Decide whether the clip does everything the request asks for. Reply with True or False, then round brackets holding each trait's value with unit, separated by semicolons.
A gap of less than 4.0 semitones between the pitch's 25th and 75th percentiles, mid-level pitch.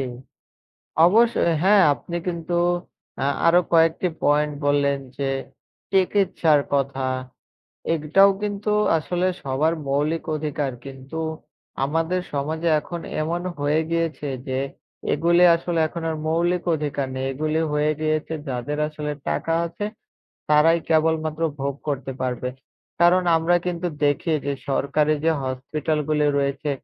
True (2.9 semitones; 155 Hz)